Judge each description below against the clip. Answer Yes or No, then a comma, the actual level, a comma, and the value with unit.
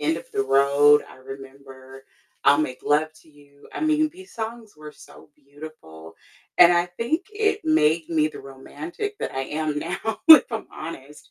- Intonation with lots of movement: Yes, wide, 8.0 semitones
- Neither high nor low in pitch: Yes, medium, 155 Hz